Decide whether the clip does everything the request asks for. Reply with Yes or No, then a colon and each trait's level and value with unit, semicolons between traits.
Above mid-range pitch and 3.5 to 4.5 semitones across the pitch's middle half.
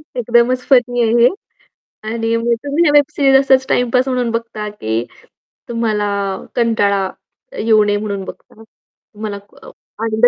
No: high, 230 Hz; narrow, 2.6 semitones